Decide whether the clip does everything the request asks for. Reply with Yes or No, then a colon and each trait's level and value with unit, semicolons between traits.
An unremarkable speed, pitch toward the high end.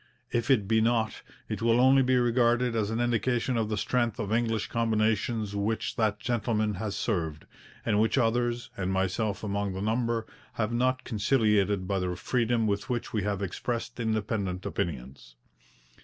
No: average, 165 wpm; low, 110 Hz